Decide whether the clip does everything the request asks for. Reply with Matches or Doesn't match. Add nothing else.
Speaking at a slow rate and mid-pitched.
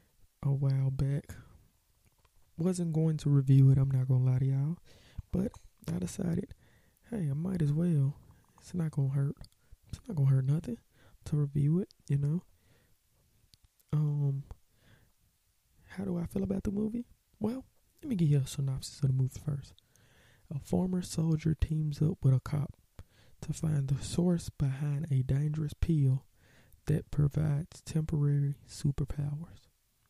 Doesn't match